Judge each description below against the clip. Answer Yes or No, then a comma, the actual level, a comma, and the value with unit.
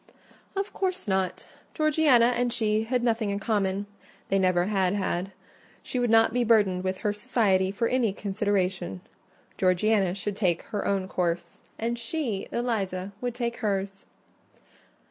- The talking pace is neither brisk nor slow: Yes, average, 145 wpm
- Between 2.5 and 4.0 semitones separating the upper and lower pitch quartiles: Yes, average, 3.7 semitones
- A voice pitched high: Yes, high, 205 Hz